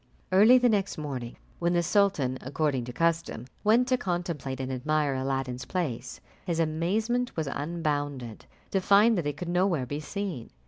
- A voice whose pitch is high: No, medium, 160 Hz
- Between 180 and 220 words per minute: No, average, 165 wpm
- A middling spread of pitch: No, wide, 6.1 semitones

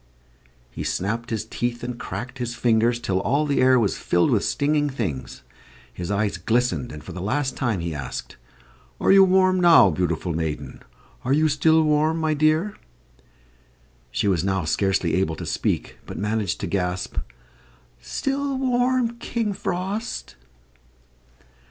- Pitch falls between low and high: No, low, 120 Hz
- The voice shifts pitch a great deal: Yes, wide, 8.8 semitones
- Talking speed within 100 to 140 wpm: No, average, 150 wpm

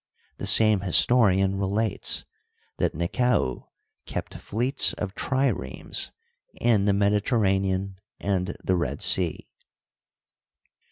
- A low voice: Yes, low, 100 Hz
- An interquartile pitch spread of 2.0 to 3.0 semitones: Yes, average, 2.7 semitones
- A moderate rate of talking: No, slow, 95 wpm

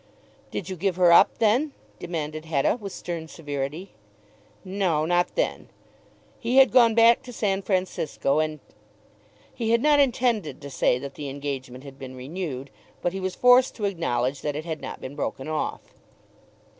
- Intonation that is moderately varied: No, wide, 6.6 semitones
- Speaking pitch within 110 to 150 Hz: No, medium, 170 Hz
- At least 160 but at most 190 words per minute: Yes, average, 170 wpm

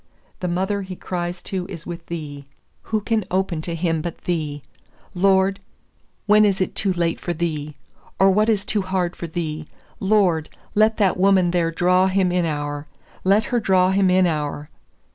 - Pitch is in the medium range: Yes, medium, 180 Hz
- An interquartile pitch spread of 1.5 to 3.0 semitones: Yes, average, 2.7 semitones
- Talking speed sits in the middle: Yes, average, 170 wpm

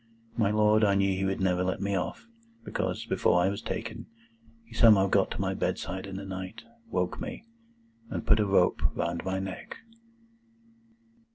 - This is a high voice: No, very low, 95 Hz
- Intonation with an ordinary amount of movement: No, narrow, 2.0 semitones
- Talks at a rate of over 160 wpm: Yes, average, 175 wpm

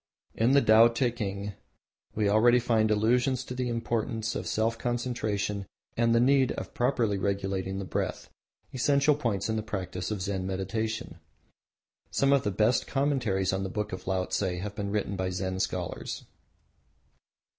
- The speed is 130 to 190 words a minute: Yes, average, 155 wpm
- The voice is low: Yes, low, 110 Hz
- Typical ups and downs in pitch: Yes, average, 3.7 semitones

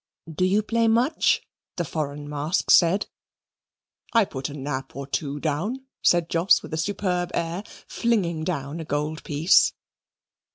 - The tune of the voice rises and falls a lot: No, average, 4.7 semitones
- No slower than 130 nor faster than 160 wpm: Yes, average, 150 wpm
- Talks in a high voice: No, medium, 165 Hz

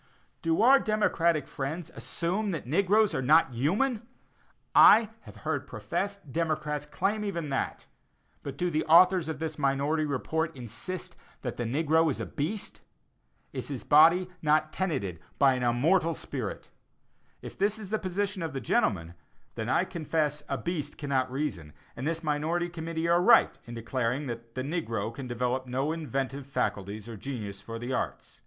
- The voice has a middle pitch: Yes, medium, 150 Hz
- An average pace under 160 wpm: No, average, 165 wpm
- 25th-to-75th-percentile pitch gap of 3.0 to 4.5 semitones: No, average, 5.0 semitones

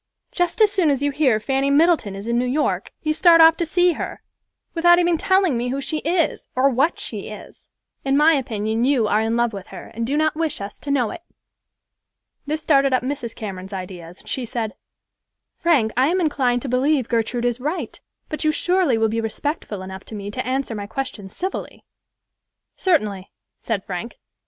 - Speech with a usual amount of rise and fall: No, wide, 5.8 semitones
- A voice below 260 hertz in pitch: No, very high, 265 Hz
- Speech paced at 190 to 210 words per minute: Yes, average, 200 wpm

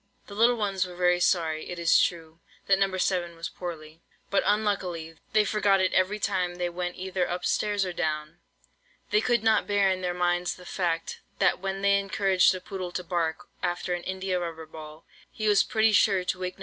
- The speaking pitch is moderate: Yes, medium, 180 Hz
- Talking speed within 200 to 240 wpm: Yes, fast, 205 wpm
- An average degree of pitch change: No, narrow, 2.2 semitones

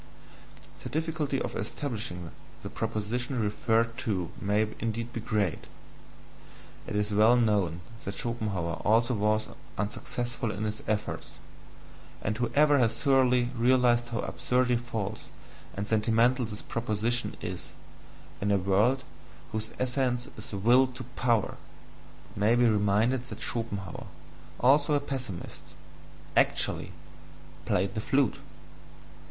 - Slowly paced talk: Yes, slow, 120 wpm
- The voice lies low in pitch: Yes, low, 115 Hz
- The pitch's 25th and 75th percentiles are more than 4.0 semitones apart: No, average, 3.0 semitones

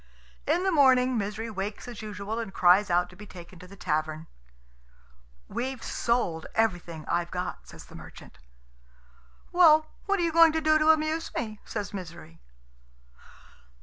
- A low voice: No, high, 215 Hz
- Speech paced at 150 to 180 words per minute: Yes, average, 155 wpm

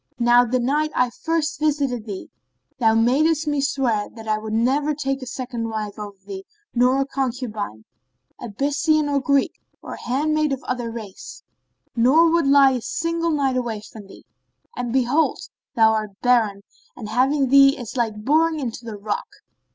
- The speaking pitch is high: Yes, very high, 250 Hz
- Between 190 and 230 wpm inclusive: No, average, 165 wpm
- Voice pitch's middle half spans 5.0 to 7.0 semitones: No, average, 4.3 semitones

